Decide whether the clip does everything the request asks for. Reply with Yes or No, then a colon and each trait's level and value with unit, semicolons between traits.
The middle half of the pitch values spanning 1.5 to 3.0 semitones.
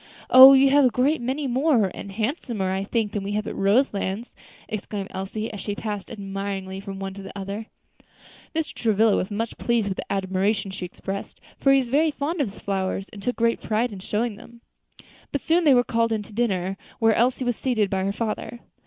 No: average, 3.8 semitones